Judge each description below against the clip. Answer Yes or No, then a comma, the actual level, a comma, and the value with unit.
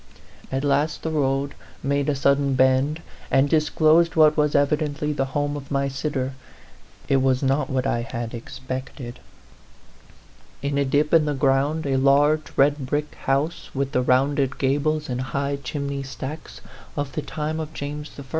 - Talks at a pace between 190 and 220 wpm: No, average, 165 wpm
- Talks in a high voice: No, medium, 140 Hz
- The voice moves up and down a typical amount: No, narrow, 1.9 semitones